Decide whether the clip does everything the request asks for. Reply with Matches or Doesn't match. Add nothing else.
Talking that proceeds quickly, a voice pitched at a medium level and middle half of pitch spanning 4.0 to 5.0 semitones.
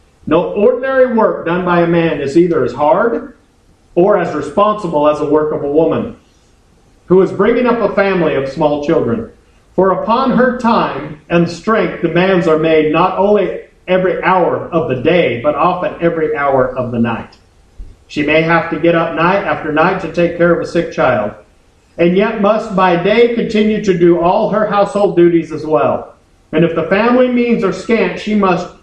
Doesn't match